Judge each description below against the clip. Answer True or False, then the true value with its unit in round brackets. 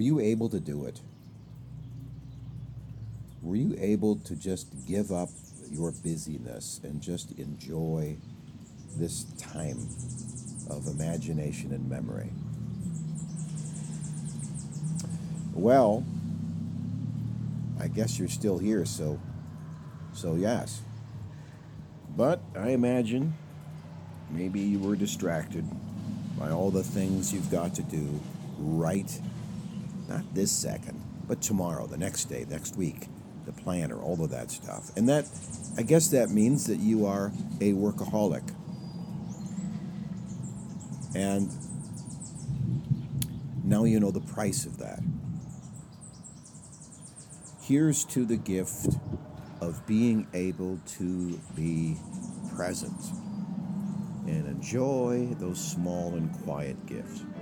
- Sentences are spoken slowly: True (110 wpm)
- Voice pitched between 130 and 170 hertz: False (120 Hz)